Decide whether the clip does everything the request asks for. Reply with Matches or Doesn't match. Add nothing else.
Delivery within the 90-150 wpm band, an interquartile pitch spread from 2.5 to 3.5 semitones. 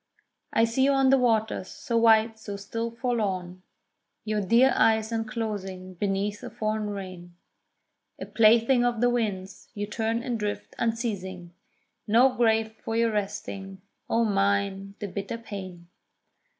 Matches